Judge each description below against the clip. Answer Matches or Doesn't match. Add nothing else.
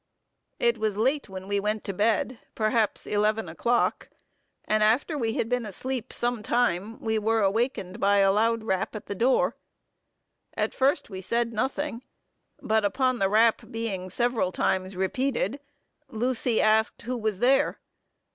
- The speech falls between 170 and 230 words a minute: Doesn't match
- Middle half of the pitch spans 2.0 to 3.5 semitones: Matches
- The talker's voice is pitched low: Doesn't match